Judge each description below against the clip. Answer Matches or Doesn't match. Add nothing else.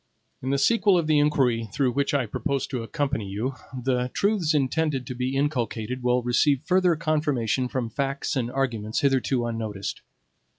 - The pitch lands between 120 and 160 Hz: Matches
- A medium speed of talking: Matches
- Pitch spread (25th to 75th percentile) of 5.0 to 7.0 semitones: Doesn't match